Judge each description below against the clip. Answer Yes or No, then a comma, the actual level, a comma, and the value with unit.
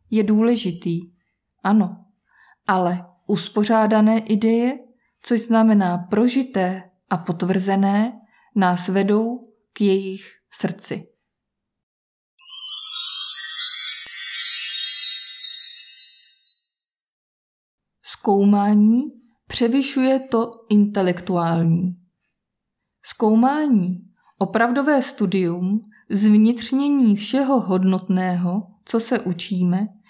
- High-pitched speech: Yes, high, 200 Hz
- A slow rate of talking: Yes, slow, 60 wpm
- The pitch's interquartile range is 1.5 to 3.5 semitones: No, average, 4.1 semitones